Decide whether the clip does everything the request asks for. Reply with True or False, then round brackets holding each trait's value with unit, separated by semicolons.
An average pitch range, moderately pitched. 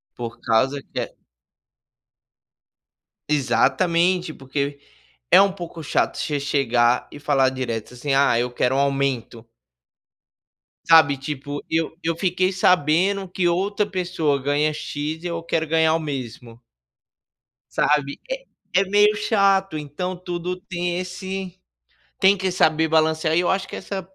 True (4.6 semitones; 160 Hz)